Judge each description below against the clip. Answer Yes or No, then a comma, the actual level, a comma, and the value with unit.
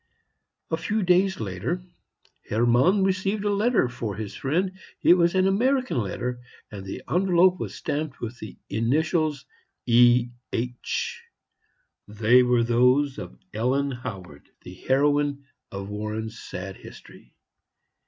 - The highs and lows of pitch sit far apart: Yes, wide, 8.2 semitones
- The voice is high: No, low, 130 Hz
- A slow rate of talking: Yes, slow, 125 wpm